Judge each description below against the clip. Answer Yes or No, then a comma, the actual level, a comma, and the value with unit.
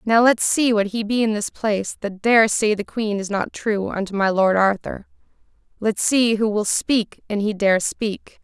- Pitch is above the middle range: Yes, high, 210 Hz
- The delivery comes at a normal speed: No, fast, 215 wpm